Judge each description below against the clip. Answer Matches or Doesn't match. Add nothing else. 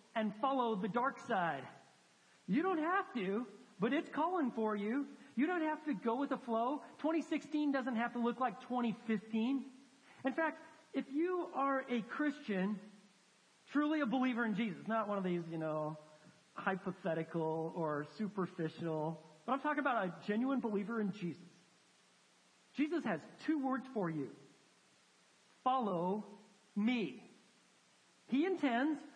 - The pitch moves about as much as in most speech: Doesn't match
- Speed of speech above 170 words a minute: Doesn't match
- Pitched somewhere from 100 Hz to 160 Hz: Doesn't match